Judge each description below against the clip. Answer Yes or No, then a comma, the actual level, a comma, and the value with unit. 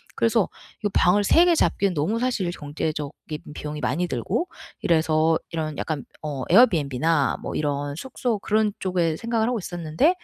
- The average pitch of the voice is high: No, medium, 170 Hz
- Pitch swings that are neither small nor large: No, wide, 6.2 semitones